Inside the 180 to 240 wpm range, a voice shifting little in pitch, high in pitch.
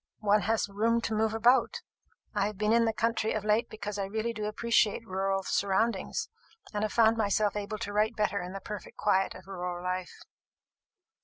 Yes: average, 190 wpm; narrow, 2.2 semitones; high, 210 Hz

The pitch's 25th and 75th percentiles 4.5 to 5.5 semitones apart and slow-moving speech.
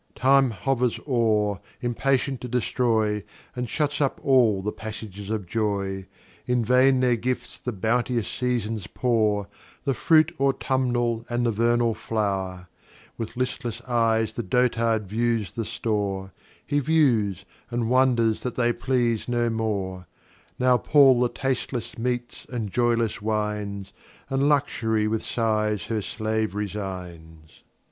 No: average, 3.0 semitones; slow, 130 wpm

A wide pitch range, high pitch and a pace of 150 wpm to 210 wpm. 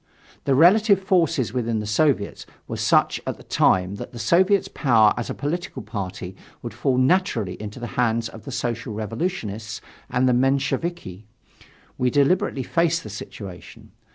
No: wide, 6.9 semitones; low, 125 Hz; average, 155 wpm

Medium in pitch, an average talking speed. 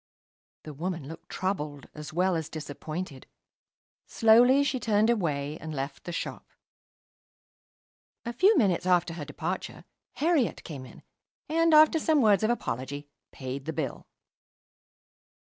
No: medium, 175 Hz; slow, 130 wpm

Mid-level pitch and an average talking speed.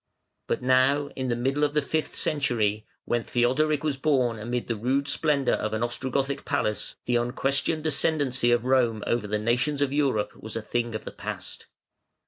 No: low, 130 Hz; average, 180 wpm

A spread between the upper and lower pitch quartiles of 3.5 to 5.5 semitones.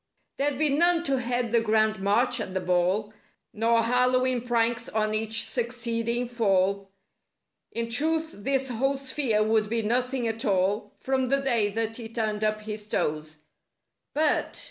No: average, 3.0 semitones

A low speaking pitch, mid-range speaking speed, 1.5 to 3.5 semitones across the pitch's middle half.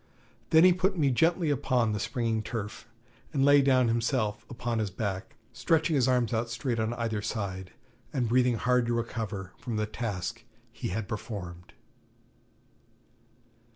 Yes: low, 115 Hz; average, 155 wpm; average, 3.2 semitones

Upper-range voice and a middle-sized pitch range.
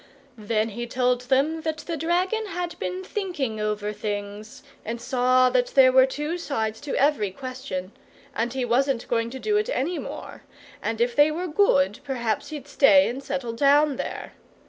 Yes: very high, 260 Hz; average, 5.0 semitones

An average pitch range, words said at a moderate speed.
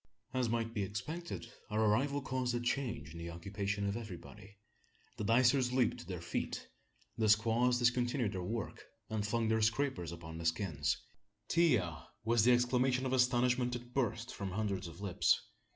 Yes: average, 4.0 semitones; average, 170 wpm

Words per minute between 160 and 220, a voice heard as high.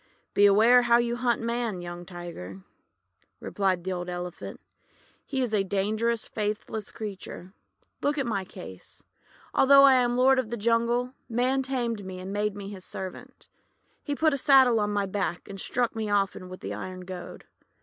Yes: average, 170 wpm; high, 210 Hz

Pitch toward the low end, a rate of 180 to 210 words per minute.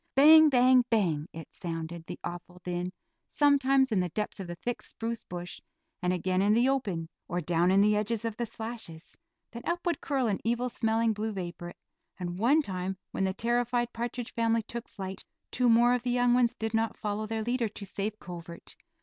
No: high, 220 Hz; average, 200 wpm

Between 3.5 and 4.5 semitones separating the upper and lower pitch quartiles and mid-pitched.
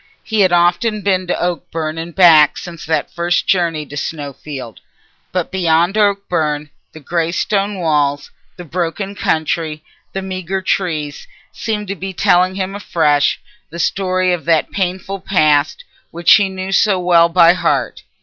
No: average, 3.1 semitones; medium, 175 Hz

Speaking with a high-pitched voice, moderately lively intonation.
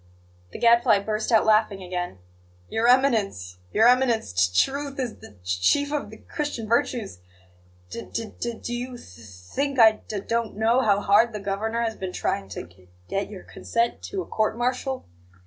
Yes: high, 220 Hz; average, 3.7 semitones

